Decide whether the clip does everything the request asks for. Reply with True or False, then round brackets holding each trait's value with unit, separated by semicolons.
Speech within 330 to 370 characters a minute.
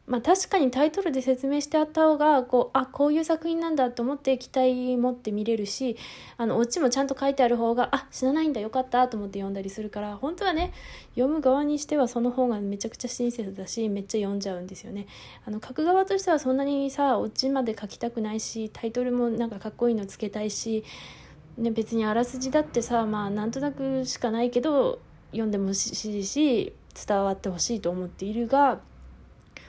True (350 characters per minute)